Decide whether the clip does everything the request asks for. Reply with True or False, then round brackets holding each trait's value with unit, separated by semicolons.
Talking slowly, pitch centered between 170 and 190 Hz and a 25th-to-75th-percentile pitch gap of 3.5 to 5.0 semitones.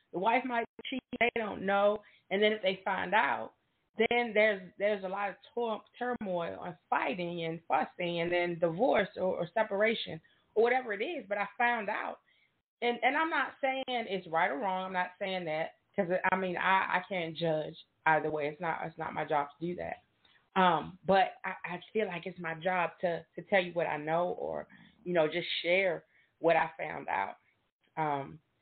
False (200 wpm; 185 Hz; 4.1 semitones)